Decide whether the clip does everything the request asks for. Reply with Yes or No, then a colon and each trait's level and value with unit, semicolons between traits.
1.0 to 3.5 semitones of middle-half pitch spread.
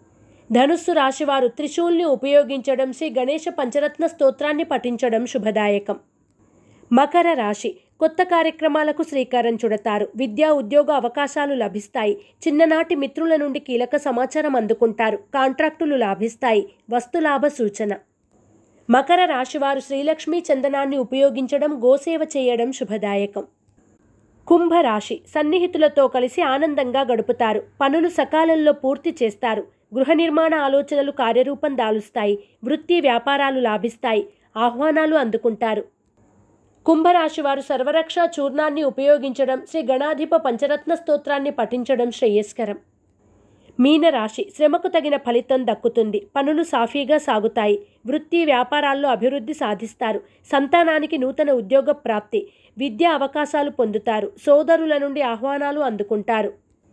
No: average, 4.7 semitones